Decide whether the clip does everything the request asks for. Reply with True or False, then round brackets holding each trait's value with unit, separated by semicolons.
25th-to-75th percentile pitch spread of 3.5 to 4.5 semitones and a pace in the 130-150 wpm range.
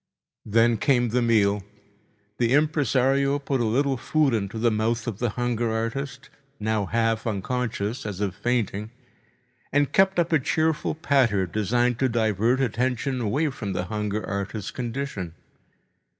True (4.0 semitones; 140 wpm)